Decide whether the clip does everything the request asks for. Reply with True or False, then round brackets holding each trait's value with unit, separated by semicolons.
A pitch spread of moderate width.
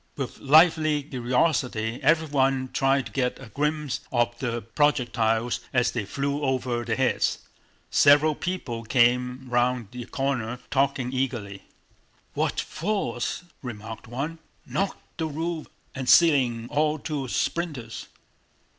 True (3.7 semitones)